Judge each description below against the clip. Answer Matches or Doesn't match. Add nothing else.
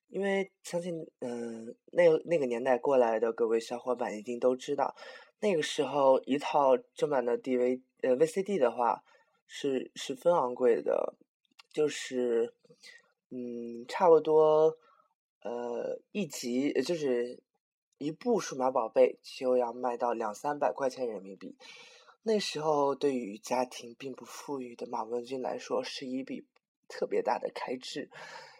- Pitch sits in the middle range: Matches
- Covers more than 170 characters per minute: Matches